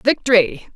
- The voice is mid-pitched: No, high, 215 Hz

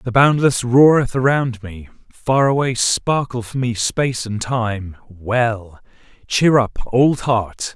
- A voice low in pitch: Yes, low, 120 Hz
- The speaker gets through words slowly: Yes, slow, 130 wpm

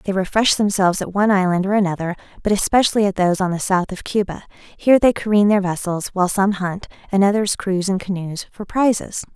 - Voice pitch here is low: No, high, 195 Hz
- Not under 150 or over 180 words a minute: No, fast, 205 wpm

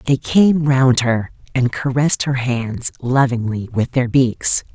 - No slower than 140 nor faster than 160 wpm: Yes, average, 150 wpm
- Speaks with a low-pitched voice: Yes, low, 130 Hz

